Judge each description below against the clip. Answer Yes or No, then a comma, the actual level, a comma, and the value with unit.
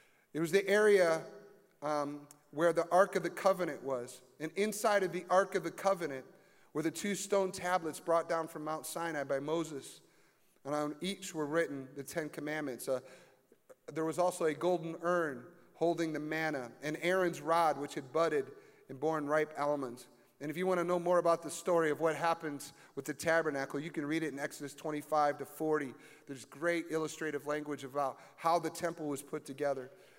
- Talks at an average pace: Yes, average, 190 wpm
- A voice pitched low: No, medium, 160 Hz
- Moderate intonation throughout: Yes, average, 3.2 semitones